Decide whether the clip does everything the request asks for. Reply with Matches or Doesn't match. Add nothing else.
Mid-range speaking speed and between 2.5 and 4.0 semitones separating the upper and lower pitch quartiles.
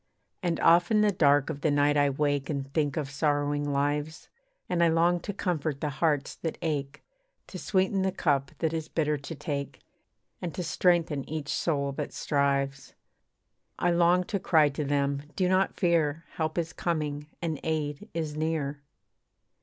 Matches